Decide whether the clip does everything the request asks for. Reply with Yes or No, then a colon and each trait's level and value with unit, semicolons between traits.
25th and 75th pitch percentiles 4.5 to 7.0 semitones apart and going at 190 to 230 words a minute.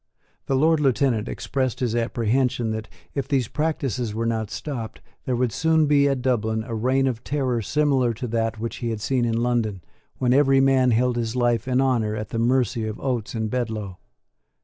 No: average, 2.9 semitones; average, 195 wpm